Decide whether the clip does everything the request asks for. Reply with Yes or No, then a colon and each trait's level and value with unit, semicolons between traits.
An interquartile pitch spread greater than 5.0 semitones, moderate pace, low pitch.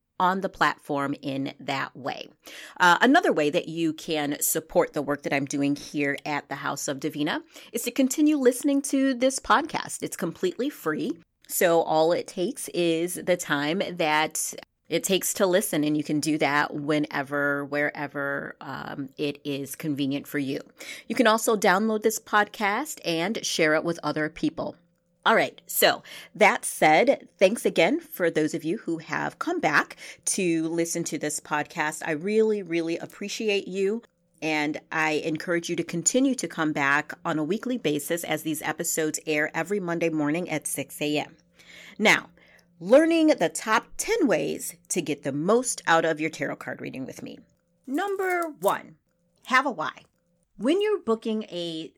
No: wide, 5.6 semitones; average, 170 wpm; medium, 170 Hz